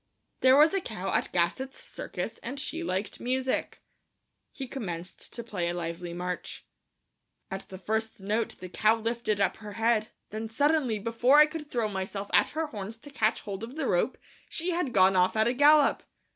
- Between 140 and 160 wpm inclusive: No, average, 185 wpm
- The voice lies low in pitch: No, high, 225 Hz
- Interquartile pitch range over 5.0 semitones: Yes, wide, 5.5 semitones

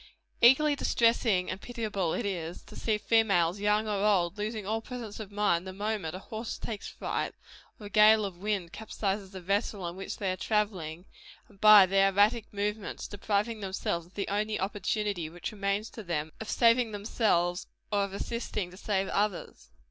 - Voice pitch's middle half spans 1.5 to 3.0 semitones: Yes, narrow, 2.5 semitones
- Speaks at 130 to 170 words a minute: No, average, 180 wpm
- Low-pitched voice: No, high, 205 Hz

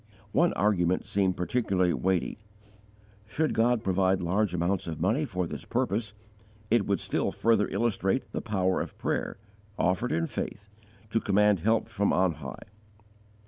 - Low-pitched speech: Yes, low, 100 Hz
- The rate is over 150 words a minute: No, average, 145 wpm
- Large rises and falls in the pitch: No, average, 3.4 semitones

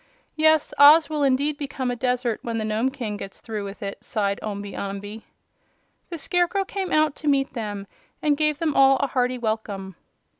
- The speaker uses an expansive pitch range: Yes, wide, 5.8 semitones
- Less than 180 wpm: No, average, 185 wpm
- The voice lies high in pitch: Yes, very high, 255 Hz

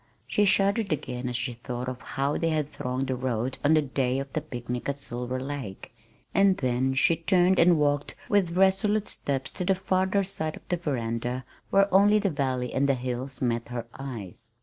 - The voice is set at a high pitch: No, medium, 140 Hz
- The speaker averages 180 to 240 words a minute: Yes, average, 195 wpm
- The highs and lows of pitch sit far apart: Yes, wide, 6.1 semitones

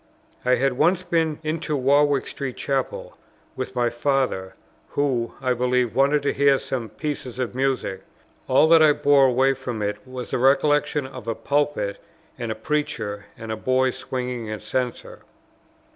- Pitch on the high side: No, low, 130 Hz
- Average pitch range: Yes, average, 3.0 semitones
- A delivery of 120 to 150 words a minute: No, average, 160 wpm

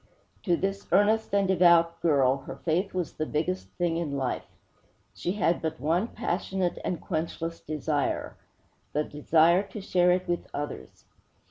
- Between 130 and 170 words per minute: Yes, average, 150 wpm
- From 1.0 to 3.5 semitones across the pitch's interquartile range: Yes, average, 2.9 semitones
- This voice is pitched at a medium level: Yes, medium, 170 Hz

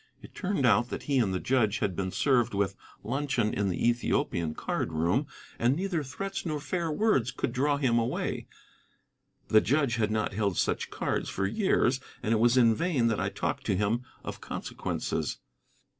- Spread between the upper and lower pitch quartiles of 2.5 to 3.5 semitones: No, average, 5.2 semitones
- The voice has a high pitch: No, low, 120 Hz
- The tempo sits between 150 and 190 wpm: Yes, average, 185 wpm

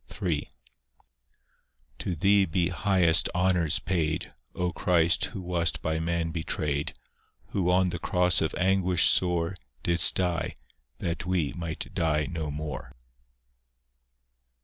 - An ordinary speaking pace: No, slow, 120 wpm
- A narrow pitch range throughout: Yes, narrow, 2.1 semitones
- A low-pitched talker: Yes, very low, 85 Hz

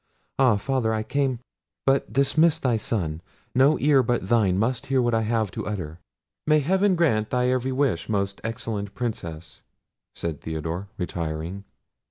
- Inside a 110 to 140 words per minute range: No, average, 150 wpm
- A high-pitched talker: No, low, 115 Hz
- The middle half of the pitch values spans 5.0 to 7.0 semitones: Yes, wide, 5.4 semitones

